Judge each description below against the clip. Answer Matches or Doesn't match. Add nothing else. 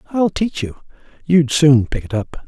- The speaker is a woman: Doesn't match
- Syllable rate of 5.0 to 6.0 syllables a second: Doesn't match